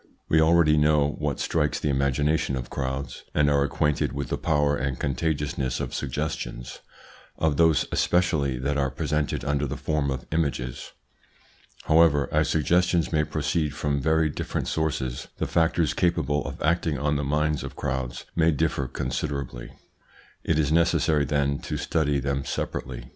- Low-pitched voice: Yes, very low, 75 Hz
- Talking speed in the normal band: Yes, average, 155 wpm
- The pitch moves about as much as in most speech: No, narrow, 2.3 semitones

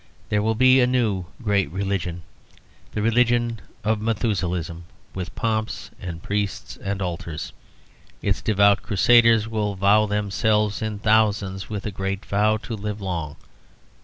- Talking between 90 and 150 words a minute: Yes, slow, 135 wpm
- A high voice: No, low, 105 Hz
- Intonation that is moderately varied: No, narrow, 2.3 semitones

